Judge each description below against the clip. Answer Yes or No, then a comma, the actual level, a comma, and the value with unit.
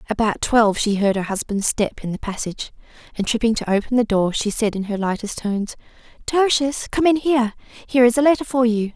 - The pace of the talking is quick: Yes, fast, 210 wpm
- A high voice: Yes, high, 230 Hz